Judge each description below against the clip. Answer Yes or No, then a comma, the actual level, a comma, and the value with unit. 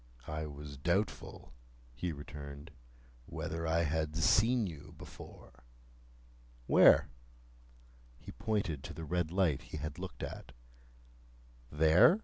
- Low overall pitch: Yes, very low, 80 Hz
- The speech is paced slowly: Yes, slow, 115 wpm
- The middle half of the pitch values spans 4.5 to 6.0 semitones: No, average, 3.3 semitones